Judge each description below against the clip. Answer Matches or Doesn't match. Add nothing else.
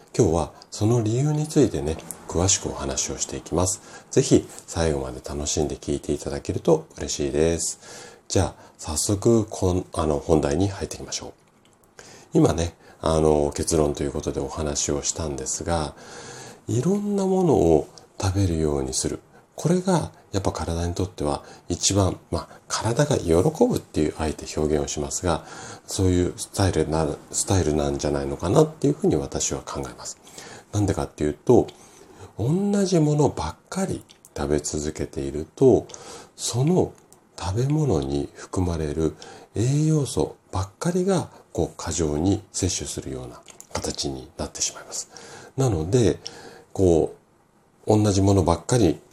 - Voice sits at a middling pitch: Doesn't match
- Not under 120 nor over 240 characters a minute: Doesn't match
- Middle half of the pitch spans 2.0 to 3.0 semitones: Doesn't match